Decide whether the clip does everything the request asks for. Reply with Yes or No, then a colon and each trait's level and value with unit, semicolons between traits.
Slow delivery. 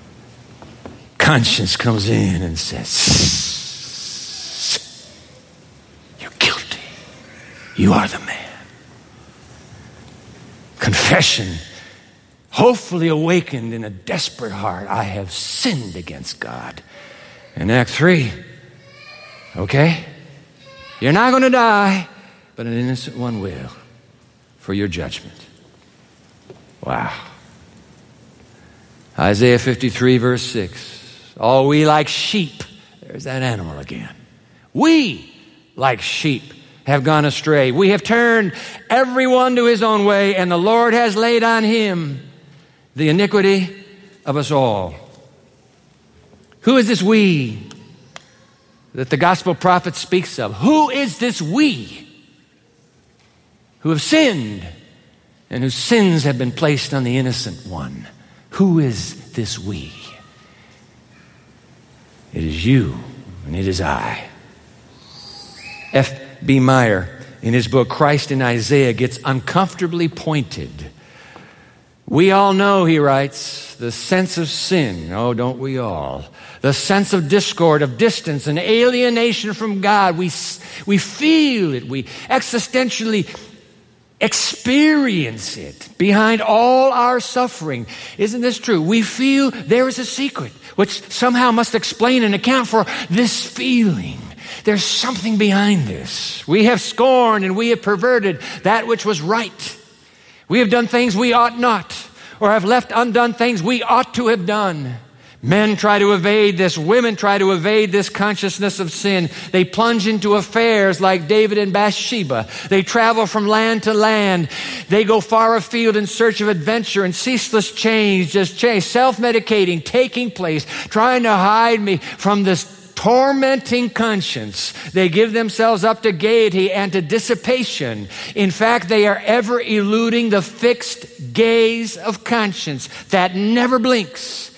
Yes: slow, 130 wpm